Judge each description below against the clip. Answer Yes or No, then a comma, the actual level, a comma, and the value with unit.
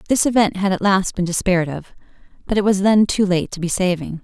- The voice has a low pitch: No, high, 190 Hz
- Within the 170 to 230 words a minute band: No, fast, 240 wpm